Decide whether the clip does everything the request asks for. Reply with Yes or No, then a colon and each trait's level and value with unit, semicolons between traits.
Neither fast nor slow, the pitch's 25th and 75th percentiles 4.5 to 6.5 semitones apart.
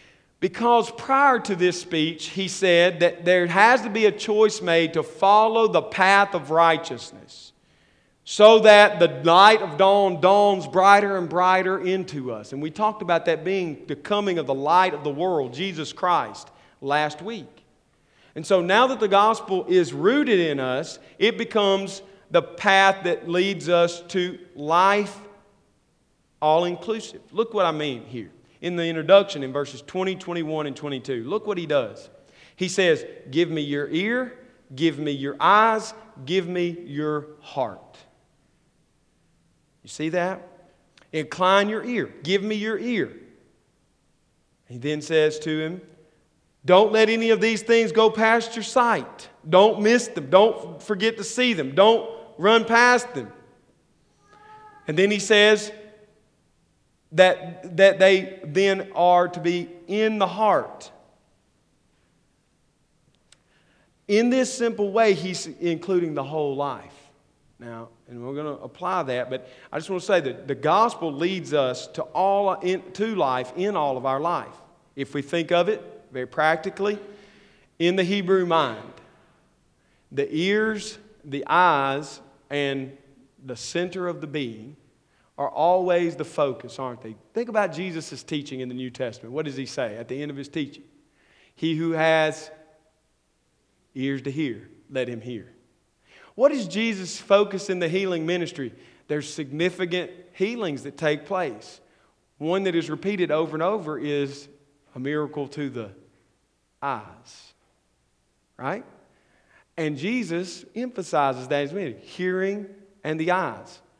Yes: average, 150 wpm; average, 5.2 semitones